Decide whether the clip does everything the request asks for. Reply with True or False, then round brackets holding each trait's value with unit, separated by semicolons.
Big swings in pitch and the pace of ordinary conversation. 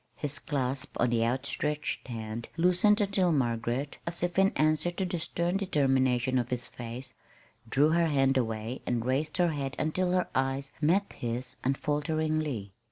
False (5.0 semitones; 160 wpm)